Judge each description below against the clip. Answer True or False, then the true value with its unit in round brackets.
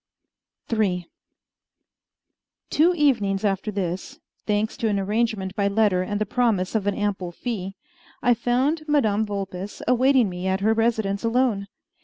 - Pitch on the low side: False (210 Hz)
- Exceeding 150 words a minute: False (140 wpm)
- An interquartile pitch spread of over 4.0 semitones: False (3.2 semitones)